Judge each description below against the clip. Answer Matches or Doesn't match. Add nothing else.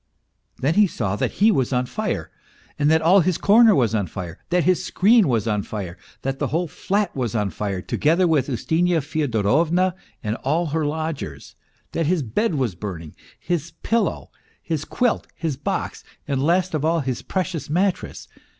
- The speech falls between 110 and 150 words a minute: Doesn't match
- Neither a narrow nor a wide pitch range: Doesn't match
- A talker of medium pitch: Matches